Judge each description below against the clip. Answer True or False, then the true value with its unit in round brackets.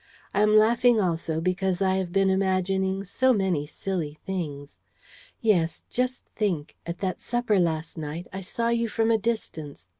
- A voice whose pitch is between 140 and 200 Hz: True (190 Hz)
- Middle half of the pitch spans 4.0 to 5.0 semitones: True (4.3 semitones)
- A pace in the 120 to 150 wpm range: False (160 wpm)